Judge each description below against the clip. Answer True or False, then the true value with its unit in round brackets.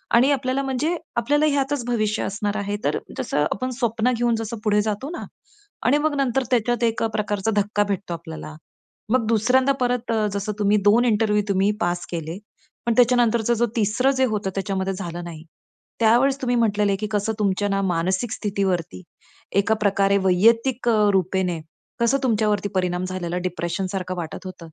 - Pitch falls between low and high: False (210 Hz)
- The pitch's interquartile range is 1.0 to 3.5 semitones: False (3.9 semitones)